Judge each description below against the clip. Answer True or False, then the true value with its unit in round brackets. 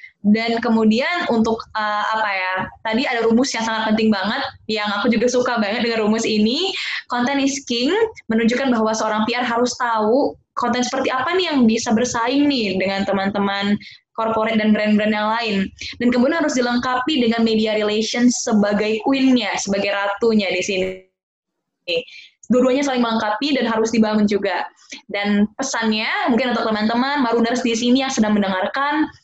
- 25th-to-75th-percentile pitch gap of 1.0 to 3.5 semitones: True (2.9 semitones)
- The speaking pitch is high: True (230 Hz)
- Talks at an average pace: False (155 wpm)